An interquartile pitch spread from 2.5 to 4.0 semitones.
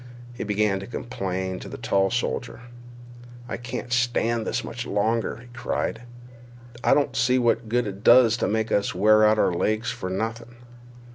Yes: average, 2.8 semitones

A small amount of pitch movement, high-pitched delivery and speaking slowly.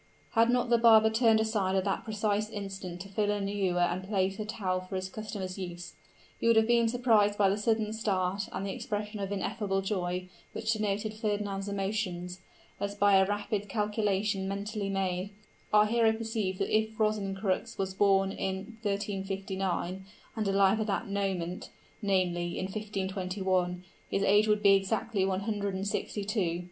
No: narrow, 2.0 semitones; high, 200 Hz; average, 170 wpm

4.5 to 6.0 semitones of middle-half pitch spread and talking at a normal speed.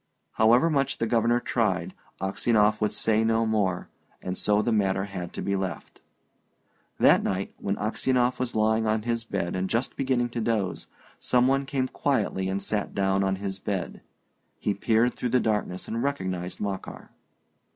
No: average, 3.6 semitones; average, 170 wpm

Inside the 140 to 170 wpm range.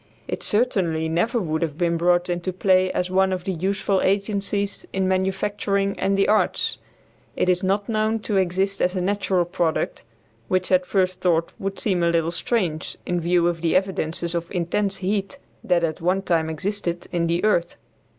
No: average, 180 wpm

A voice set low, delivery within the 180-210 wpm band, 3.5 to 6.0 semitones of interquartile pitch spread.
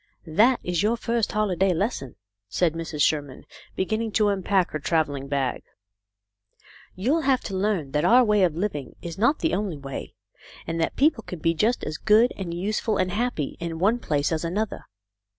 No: medium, 185 Hz; average, 185 wpm; wide, 5.5 semitones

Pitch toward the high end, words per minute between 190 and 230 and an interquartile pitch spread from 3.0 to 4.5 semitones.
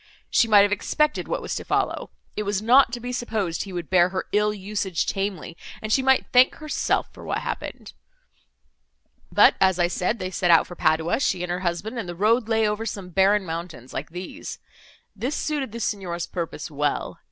Yes: high, 195 Hz; average, 200 wpm; average, 4.2 semitones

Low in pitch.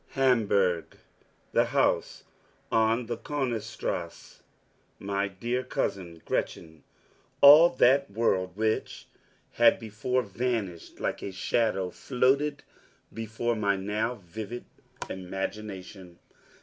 Yes: low, 110 Hz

